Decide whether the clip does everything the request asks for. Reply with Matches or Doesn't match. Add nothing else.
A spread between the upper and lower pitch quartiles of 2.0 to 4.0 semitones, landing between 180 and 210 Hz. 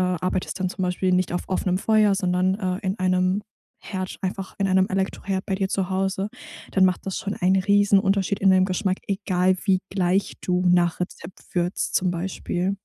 Doesn't match